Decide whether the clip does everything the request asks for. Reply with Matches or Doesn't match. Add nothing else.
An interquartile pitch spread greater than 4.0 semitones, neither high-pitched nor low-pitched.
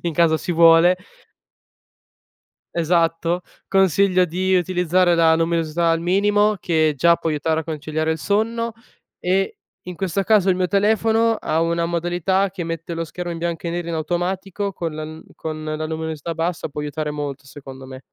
Doesn't match